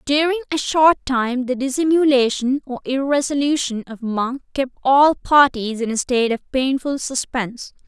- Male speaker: No, female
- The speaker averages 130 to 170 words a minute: Yes, average, 145 wpm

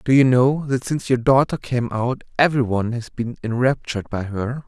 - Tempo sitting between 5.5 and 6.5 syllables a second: No, 5.3 syllables/s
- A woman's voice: No, male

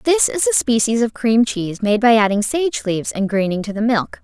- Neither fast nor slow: No, fast, 240 wpm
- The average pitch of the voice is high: Yes, high, 230 Hz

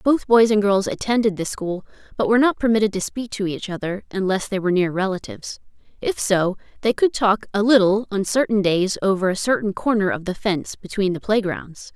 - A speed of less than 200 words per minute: No, fast, 205 wpm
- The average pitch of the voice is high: Yes, high, 205 Hz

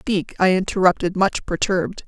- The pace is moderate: Yes, average, 145 wpm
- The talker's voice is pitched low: No, medium, 185 Hz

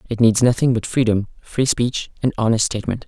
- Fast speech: No, average, 195 wpm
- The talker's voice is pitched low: Yes, low, 115 Hz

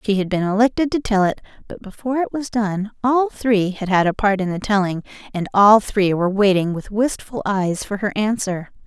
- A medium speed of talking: No, fast, 215 wpm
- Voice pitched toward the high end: Yes, high, 205 Hz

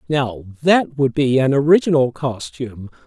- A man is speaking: Yes, male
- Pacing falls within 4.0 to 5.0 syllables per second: Yes, 4.4 syllables/s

